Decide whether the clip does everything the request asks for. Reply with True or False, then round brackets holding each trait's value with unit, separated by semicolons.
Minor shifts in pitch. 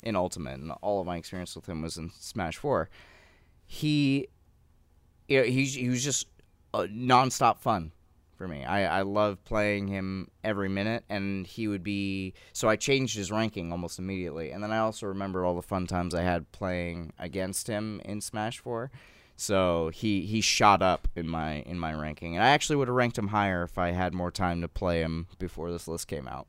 False (3.7 semitones)